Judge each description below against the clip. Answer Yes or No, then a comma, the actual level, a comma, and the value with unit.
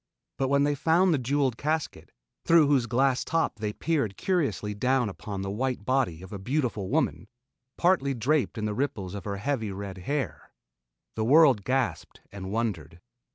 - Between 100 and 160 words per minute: No, average, 170 wpm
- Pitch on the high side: No, low, 125 Hz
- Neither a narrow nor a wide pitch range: No, wide, 5.7 semitones